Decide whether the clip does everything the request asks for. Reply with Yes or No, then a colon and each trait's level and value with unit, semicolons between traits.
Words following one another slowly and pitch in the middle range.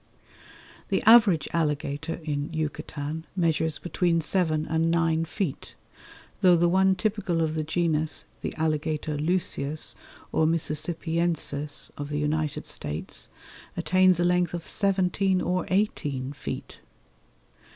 Yes: slow, 120 wpm; medium, 160 Hz